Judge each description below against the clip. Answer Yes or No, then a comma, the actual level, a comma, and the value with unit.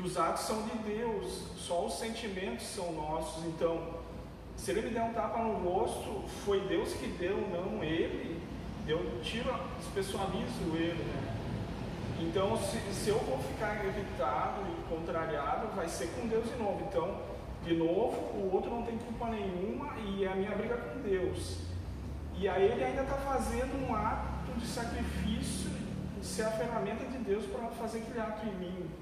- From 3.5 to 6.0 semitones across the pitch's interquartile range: Yes, wide, 5.4 semitones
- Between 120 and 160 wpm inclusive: No, average, 170 wpm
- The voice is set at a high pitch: Yes, high, 200 Hz